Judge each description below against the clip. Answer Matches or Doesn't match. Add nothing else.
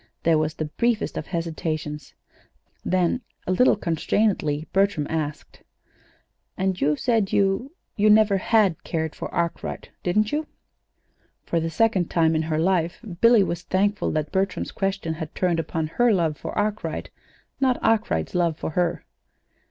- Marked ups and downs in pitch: Doesn't match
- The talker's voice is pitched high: Doesn't match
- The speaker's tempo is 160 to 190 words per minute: Doesn't match